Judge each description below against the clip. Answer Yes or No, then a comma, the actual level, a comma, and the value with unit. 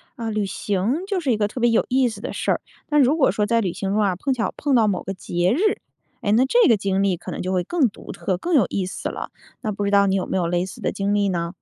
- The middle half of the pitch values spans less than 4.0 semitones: No, average, 4.4 semitones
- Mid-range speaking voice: No, high, 205 Hz